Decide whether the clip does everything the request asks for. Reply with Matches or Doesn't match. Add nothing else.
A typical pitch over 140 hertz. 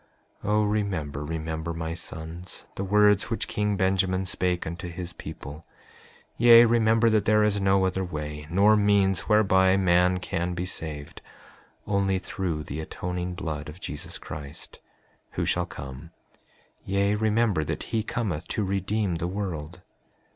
Doesn't match